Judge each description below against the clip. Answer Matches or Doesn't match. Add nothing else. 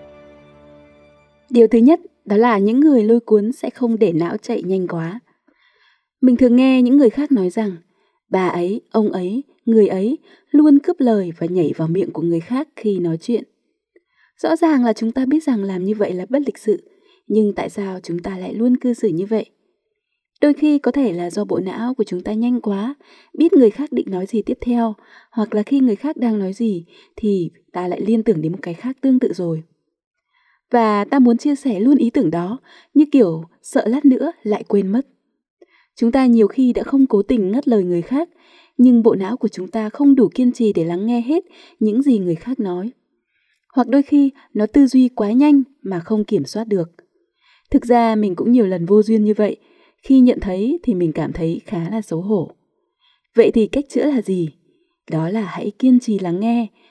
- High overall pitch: Matches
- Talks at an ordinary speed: Matches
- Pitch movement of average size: Doesn't match